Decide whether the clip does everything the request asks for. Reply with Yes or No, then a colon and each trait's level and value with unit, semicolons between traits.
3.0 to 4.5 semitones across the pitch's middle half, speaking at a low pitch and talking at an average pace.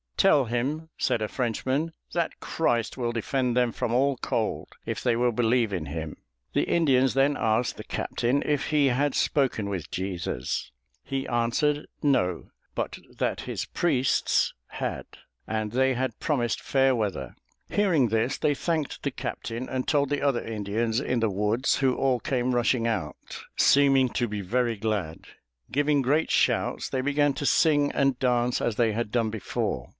Yes: average, 3.7 semitones; low, 125 Hz; average, 165 wpm